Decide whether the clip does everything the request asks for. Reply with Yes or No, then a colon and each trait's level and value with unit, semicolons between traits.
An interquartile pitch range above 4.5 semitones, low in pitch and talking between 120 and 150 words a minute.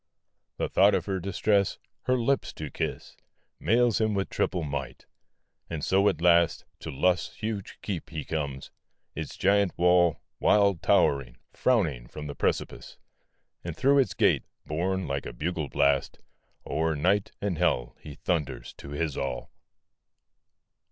Yes: average, 5.2 semitones; very low, 85 Hz; average, 145 wpm